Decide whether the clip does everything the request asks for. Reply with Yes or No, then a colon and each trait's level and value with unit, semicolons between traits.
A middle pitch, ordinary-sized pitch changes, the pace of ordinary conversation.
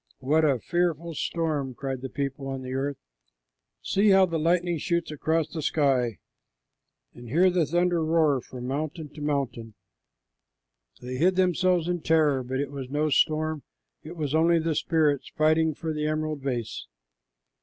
Yes: medium, 155 Hz; average, 3.4 semitones; average, 160 wpm